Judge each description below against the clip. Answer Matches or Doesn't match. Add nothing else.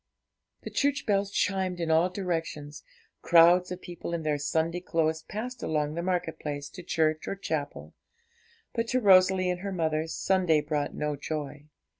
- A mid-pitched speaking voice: Matches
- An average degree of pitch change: Matches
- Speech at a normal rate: Matches